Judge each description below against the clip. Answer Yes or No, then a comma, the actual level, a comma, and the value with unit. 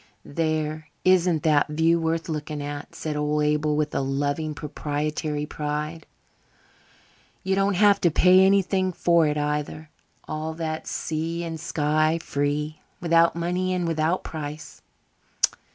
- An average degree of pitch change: No, narrow, 2.1 semitones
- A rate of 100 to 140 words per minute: Yes, slow, 135 wpm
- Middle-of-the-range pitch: Yes, medium, 155 Hz